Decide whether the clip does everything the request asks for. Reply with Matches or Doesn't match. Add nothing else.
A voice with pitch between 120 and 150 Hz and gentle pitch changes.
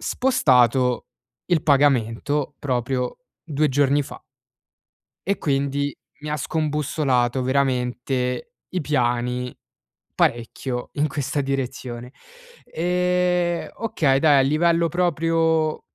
Doesn't match